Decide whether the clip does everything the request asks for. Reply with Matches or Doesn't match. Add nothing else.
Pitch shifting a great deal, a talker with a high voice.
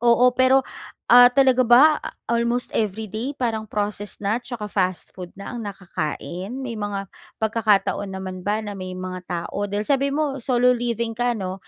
Doesn't match